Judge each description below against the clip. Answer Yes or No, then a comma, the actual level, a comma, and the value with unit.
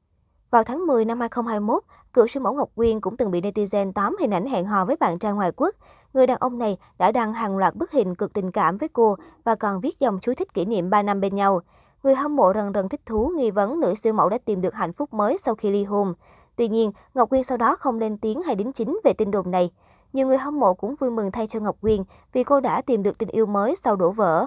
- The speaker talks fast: Yes, fast, 270 wpm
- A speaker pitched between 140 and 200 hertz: No, high, 220 Hz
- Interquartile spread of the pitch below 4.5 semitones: Yes, average, 4.0 semitones